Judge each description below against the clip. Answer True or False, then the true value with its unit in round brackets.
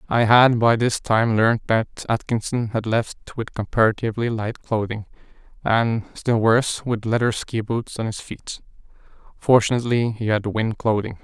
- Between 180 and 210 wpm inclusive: False (155 wpm)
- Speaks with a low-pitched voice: True (115 Hz)